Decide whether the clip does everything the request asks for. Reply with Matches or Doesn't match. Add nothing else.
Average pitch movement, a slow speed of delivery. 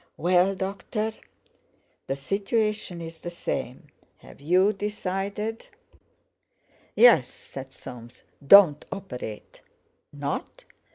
Doesn't match